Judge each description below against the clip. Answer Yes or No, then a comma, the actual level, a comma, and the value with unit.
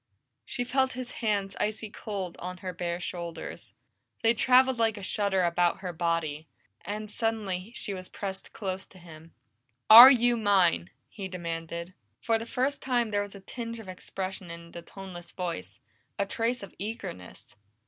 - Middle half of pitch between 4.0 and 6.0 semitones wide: Yes, average, 4.4 semitones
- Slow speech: No, average, 165 wpm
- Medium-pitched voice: No, high, 195 Hz